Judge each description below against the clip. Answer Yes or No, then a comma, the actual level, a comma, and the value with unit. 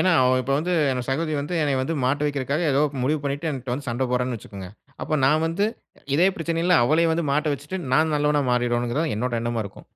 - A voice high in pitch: No, medium, 140 Hz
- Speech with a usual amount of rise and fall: Yes, average, 4.0 semitones